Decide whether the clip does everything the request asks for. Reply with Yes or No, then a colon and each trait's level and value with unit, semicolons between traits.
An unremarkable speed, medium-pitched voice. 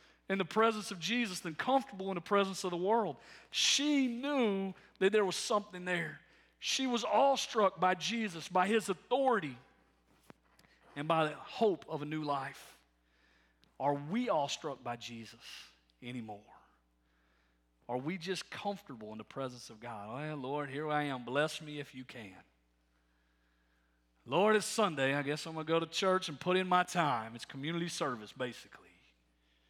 Yes: average, 170 wpm; medium, 150 Hz